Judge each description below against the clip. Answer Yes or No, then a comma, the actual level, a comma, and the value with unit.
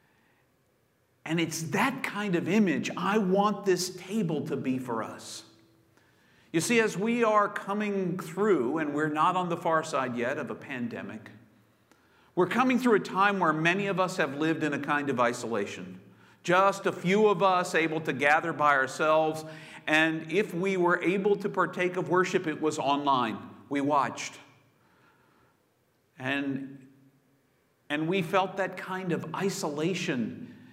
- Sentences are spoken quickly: No, average, 155 wpm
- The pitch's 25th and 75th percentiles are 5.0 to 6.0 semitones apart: Yes, wide, 5.6 semitones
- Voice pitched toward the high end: No, medium, 160 Hz